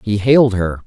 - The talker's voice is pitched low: Yes, low, 110 Hz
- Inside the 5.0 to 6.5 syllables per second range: Yes, 5.2 syllables/s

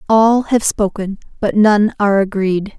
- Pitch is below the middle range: No, high, 205 Hz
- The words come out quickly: No, average, 150 wpm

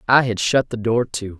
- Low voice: Yes, low, 115 Hz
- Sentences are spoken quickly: Yes, fast, 260 wpm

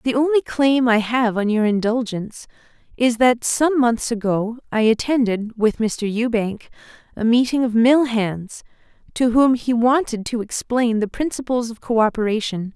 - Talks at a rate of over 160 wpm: No, average, 155 wpm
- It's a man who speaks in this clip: No, female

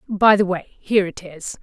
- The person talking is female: Yes, female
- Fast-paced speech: Yes, fast, 220 wpm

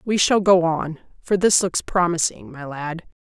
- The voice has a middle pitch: Yes, medium, 175 Hz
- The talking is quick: No, average, 185 wpm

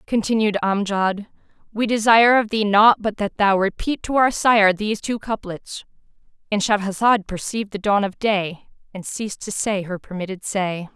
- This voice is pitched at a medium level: No, high, 205 Hz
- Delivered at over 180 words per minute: No, average, 165 wpm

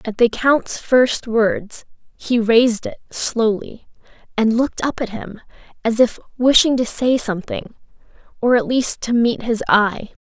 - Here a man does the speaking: No, female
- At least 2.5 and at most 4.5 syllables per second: Yes, 4.2 syllables/s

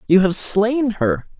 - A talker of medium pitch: No, high, 210 Hz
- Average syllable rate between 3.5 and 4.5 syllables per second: Yes, 3.6 syllables/s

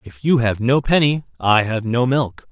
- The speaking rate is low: No, fast, 215 wpm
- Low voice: Yes, low, 125 Hz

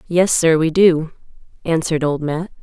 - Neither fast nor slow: Yes, average, 160 wpm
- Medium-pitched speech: Yes, medium, 165 Hz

